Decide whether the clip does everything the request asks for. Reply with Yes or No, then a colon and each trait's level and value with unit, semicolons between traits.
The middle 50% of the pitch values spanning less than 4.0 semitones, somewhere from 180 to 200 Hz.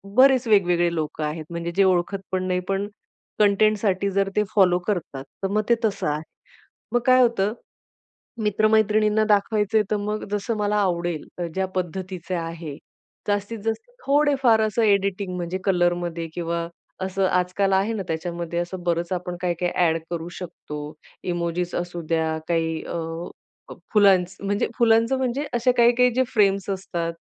Yes: average, 3.6 semitones; high, 190 Hz